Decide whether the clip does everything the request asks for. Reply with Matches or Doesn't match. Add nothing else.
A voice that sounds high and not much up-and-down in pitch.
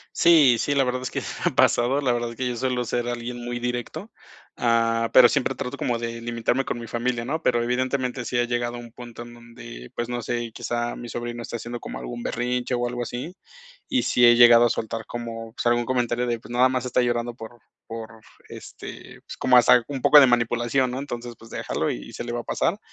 Doesn't match